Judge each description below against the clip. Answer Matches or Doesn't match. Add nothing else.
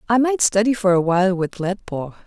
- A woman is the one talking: Matches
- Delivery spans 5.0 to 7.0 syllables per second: Matches